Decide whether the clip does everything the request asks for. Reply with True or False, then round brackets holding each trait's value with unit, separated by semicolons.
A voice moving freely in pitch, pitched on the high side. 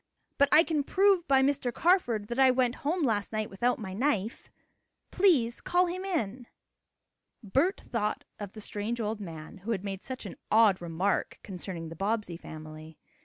True (6.2 semitones; 225 Hz)